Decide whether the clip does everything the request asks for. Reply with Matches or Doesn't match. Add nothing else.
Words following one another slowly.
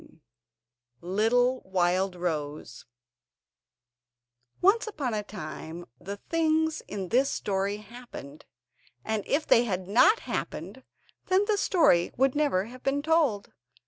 Matches